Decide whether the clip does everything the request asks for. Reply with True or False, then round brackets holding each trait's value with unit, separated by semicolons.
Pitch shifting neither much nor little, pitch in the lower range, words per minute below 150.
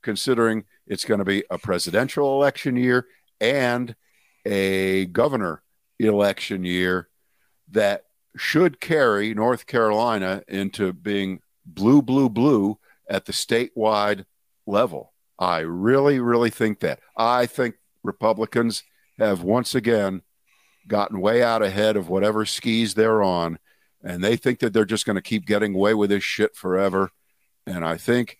True (3.3 semitones; 110 Hz; 140 wpm)